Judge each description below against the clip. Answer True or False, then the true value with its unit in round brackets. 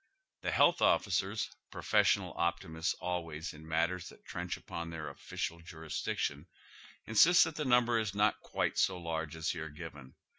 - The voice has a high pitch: False (85 Hz)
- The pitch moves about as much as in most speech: True (3.7 semitones)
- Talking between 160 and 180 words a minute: False (150 wpm)